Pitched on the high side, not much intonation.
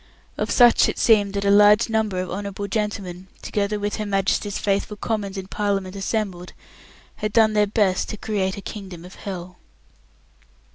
Yes: high, 200 Hz; narrow, 1.7 semitones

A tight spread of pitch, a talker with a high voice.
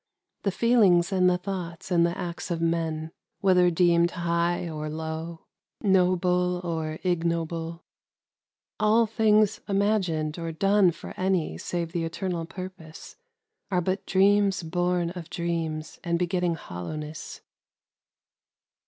No: narrow, 2.2 semitones; medium, 175 Hz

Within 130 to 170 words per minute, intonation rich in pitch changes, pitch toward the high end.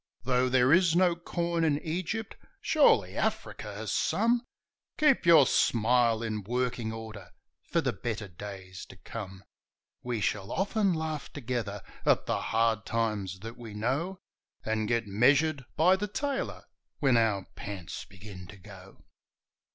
No: average, 145 wpm; wide, 7.6 semitones; low, 120 Hz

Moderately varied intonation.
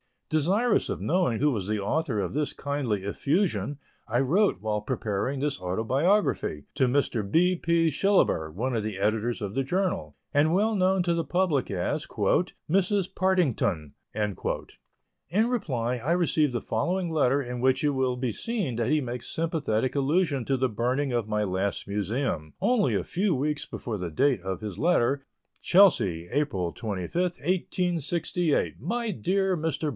No: wide, 8.0 semitones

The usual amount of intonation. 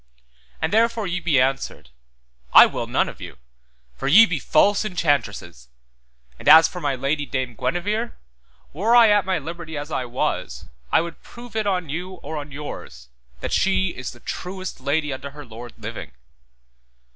No: wide, 5.8 semitones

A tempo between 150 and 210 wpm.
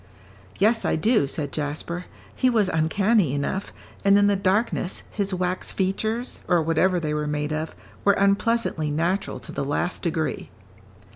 Yes: average, 155 wpm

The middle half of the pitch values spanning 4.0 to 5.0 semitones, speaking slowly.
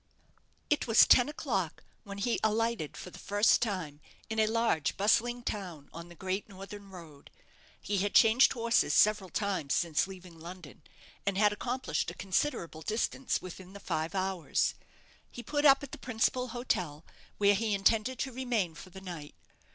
No: average, 4.4 semitones; average, 165 wpm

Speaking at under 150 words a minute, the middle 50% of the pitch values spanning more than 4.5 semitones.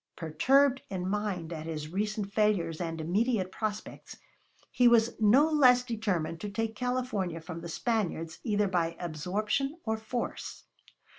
Yes: average, 140 wpm; wide, 5.5 semitones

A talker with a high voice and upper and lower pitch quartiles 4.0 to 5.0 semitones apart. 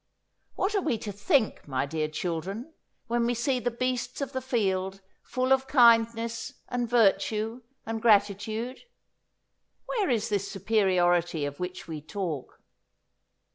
Yes: high, 220 Hz; average, 4.5 semitones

